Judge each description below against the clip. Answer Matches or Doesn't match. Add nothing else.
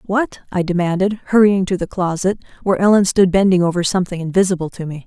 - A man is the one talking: Doesn't match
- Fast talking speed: Doesn't match